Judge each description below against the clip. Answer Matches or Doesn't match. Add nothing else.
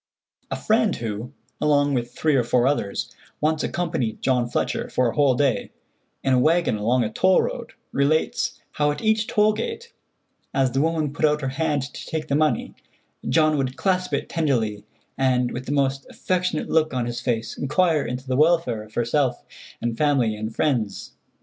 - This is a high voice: Doesn't match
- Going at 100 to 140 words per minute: Doesn't match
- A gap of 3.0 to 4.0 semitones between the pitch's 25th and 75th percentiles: Doesn't match